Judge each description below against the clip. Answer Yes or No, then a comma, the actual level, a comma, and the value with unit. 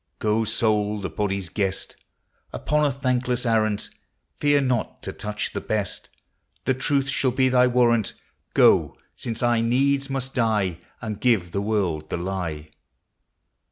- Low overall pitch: Yes, low, 115 Hz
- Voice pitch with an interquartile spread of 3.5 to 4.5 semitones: Yes, average, 4.2 semitones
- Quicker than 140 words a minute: Yes, average, 150 wpm